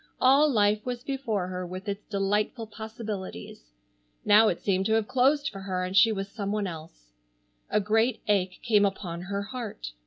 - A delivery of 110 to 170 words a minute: No, average, 180 wpm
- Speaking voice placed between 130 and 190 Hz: No, high, 205 Hz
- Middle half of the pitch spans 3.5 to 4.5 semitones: No, average, 2.9 semitones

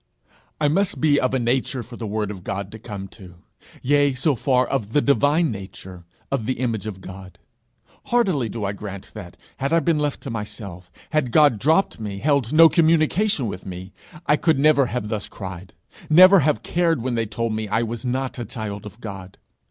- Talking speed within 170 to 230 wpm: Yes, average, 200 wpm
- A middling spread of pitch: No, wide, 6.2 semitones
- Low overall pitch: Yes, low, 120 Hz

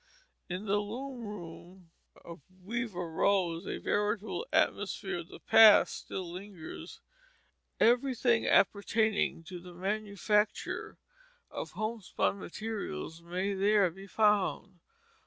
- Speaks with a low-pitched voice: No, high, 200 Hz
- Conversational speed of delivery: No, slow, 105 wpm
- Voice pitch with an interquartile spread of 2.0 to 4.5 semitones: Yes, average, 3.2 semitones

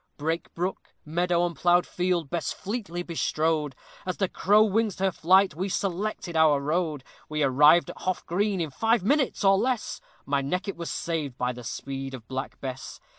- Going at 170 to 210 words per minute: Yes, average, 180 wpm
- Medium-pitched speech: Yes, medium, 170 Hz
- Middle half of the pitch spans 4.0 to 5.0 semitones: Yes, average, 4.5 semitones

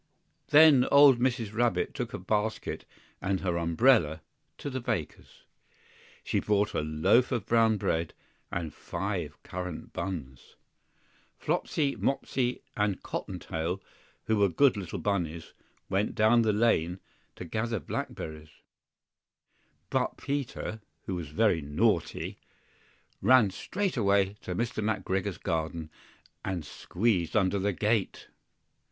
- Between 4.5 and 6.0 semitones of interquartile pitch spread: Yes, wide, 5.4 semitones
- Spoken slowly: Yes, slow, 120 wpm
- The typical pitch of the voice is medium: No, low, 100 Hz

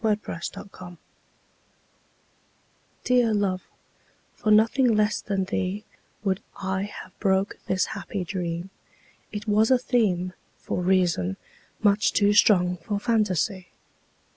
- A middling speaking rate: No, slow, 100 wpm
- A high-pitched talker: Yes, high, 200 Hz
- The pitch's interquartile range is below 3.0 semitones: Yes, narrow, 2.6 semitones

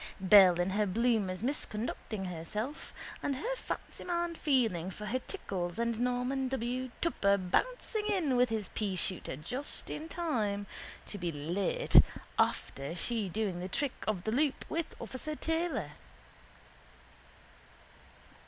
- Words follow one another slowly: Yes, slow, 125 wpm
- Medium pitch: No, high, 225 Hz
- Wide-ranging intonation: Yes, wide, 6.6 semitones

